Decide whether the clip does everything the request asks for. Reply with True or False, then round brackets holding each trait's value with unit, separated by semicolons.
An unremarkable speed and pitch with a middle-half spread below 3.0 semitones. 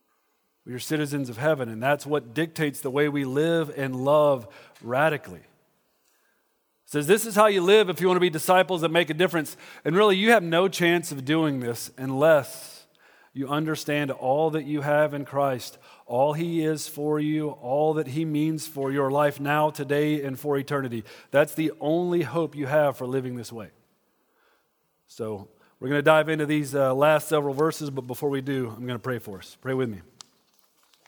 True (195 wpm; 2.5 semitones)